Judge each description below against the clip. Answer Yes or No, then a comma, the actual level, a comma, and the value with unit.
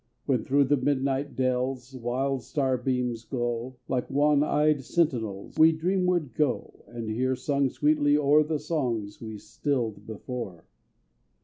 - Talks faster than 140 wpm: No, slow, 135 wpm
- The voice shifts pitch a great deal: No, average, 3.3 semitones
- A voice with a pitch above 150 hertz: No, low, 130 Hz